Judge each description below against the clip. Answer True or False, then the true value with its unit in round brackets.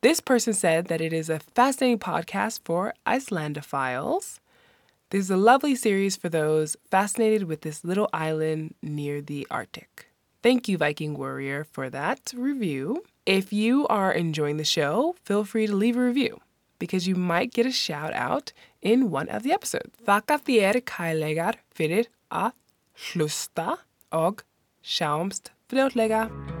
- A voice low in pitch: False (195 Hz)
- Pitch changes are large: True (7.1 semitones)